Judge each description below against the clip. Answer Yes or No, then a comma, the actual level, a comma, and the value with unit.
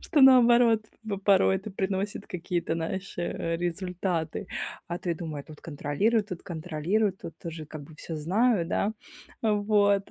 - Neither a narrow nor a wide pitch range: Yes, average, 3.9 semitones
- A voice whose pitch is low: No, medium, 185 Hz